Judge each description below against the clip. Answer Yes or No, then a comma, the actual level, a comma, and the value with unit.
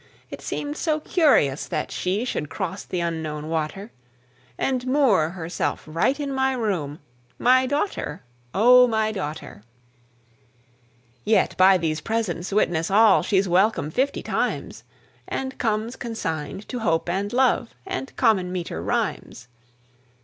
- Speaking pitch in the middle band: No, high, 205 Hz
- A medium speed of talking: No, slow, 130 wpm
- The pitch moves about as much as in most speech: No, wide, 7.1 semitones